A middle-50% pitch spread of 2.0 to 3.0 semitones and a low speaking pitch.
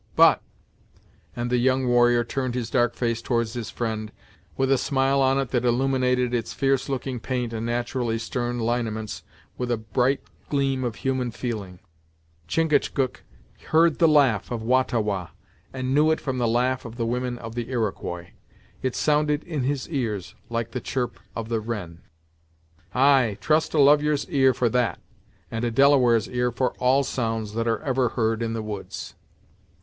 Yes: narrow, 2.6 semitones; low, 125 Hz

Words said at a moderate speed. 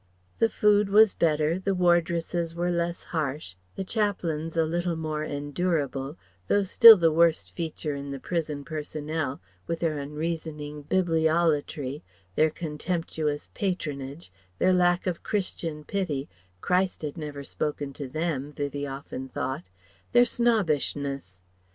No: slow, 130 wpm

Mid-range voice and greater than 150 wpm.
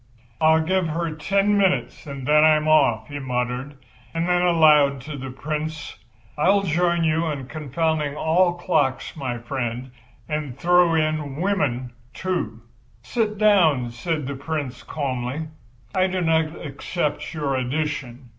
No: medium, 155 Hz; average, 145 wpm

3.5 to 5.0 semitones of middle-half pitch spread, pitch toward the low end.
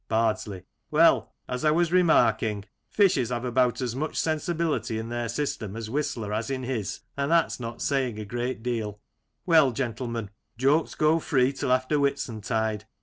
Yes: average, 4.2 semitones; low, 125 Hz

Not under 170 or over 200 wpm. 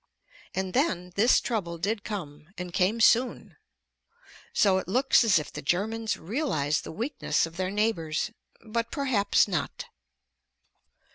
No: slow, 135 wpm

